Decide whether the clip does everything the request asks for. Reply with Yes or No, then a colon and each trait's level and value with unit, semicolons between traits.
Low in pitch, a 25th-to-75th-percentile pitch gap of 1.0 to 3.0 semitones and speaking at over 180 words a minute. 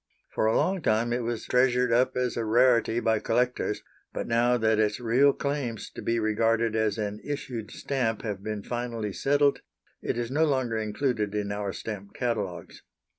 No: low, 115 Hz; narrow, 2.5 semitones; average, 175 wpm